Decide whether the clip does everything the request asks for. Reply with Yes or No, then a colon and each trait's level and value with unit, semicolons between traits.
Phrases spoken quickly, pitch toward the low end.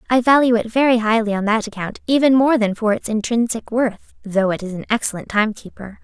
No: fast, 220 wpm; high, 225 Hz